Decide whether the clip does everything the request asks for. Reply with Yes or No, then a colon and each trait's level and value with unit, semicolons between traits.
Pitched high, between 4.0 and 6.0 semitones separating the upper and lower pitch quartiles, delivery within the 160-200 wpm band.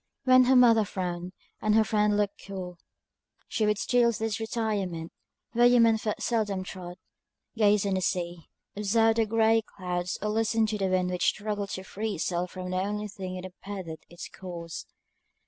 No: high, 205 Hz; average, 3.3 semitones; average, 180 wpm